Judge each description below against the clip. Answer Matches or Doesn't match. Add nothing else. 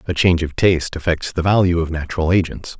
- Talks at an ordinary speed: Doesn't match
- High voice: Doesn't match